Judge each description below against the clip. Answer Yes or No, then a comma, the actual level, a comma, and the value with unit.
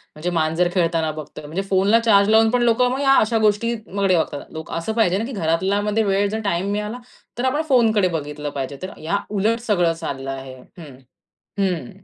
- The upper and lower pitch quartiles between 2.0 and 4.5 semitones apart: No, wide, 5.4 semitones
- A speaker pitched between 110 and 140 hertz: No, high, 195 Hz